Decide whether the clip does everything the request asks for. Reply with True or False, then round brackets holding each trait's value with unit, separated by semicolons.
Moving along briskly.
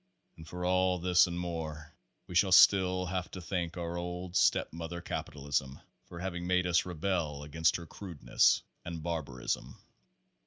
False (155 wpm)